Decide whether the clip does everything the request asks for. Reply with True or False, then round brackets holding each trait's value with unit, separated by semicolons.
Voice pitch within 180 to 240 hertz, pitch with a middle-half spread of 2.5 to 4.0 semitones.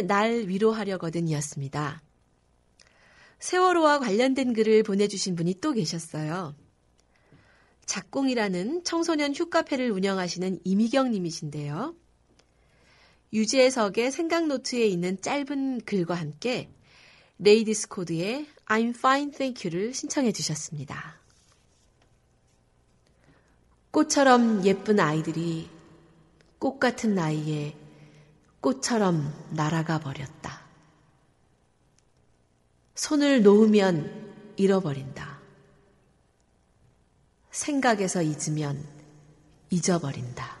False (185 Hz; 7.8 semitones)